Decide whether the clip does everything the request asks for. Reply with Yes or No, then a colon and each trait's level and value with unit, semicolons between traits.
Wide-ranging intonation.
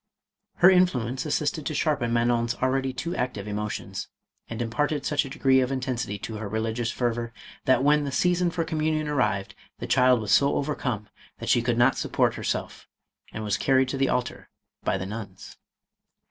No: average, 4.0 semitones